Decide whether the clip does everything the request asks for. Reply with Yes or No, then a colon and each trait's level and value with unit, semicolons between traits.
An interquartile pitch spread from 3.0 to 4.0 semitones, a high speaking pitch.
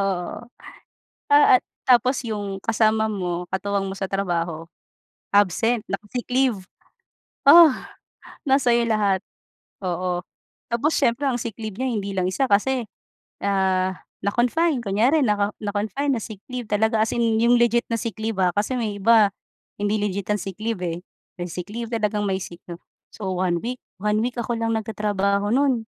Yes: average, 3.5 semitones; high, 215 Hz